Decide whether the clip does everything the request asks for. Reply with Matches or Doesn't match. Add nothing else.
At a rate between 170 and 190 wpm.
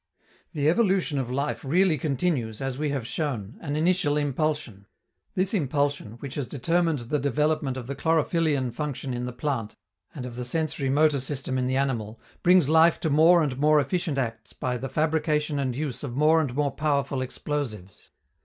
Matches